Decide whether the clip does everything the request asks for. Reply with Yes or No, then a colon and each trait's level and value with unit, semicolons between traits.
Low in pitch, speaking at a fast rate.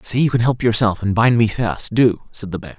Yes: low, 110 Hz; fast, 280 wpm